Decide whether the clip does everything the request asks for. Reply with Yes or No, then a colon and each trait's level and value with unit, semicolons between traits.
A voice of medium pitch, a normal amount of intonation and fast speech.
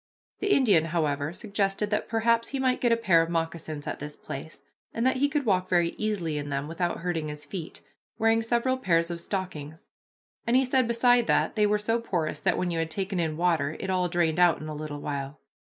No: medium, 180 Hz; wide, 6.1 semitones; fast, 220 wpm